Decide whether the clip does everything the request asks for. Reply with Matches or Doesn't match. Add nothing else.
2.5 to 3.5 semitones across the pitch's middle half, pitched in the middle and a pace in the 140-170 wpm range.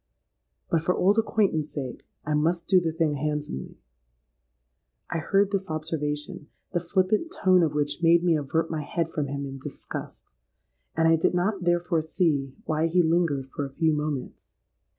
Matches